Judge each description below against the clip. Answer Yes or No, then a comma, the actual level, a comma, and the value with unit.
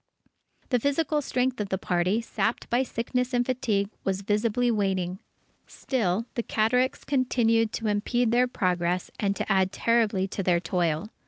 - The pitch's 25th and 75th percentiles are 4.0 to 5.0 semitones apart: Yes, average, 4.4 semitones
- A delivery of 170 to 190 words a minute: No, average, 155 wpm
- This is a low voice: No, high, 220 Hz